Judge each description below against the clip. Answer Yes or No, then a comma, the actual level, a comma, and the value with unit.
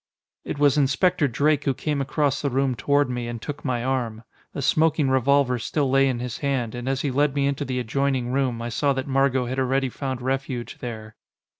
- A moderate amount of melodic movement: No, narrow, 2.2 semitones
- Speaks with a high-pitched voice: No, low, 135 Hz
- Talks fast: Yes, fast, 210 wpm